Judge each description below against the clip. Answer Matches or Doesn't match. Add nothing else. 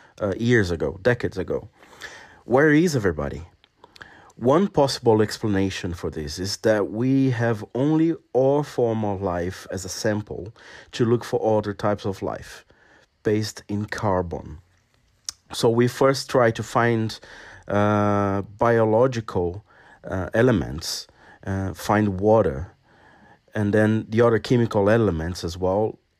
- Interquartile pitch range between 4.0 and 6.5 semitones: Doesn't match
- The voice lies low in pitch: Matches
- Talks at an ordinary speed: Doesn't match